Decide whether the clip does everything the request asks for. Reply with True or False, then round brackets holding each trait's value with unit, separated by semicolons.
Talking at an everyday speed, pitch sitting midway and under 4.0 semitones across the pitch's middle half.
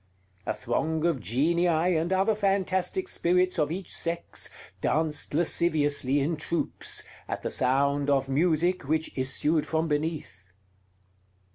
False (125 wpm; 160 Hz; 3.3 semitones)